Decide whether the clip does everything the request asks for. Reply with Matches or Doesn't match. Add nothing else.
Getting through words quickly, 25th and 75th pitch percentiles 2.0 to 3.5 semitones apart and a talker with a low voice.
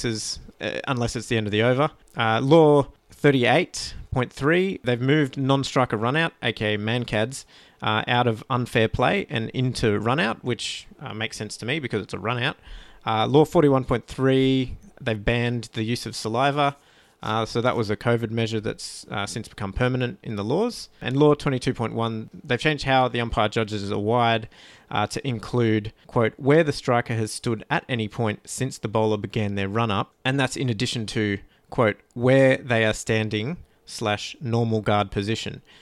Doesn't match